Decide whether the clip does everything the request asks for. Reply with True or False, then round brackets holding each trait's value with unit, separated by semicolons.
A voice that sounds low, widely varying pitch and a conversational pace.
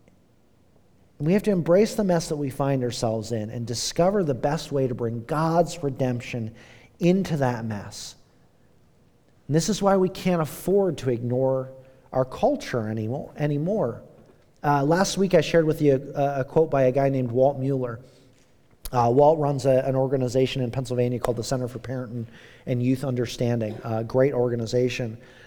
False (130 Hz; 3.5 semitones; 165 wpm)